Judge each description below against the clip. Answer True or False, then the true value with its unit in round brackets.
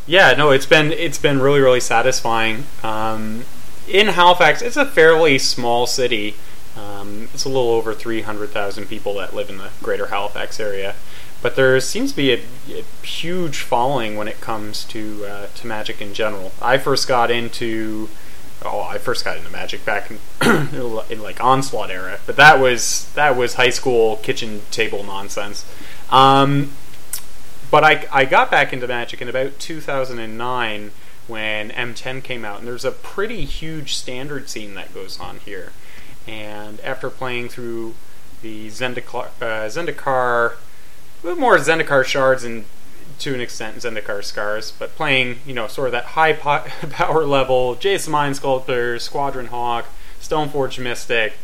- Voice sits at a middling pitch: False (125 Hz)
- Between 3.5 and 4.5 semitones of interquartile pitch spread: True (4.2 semitones)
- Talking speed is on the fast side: False (165 wpm)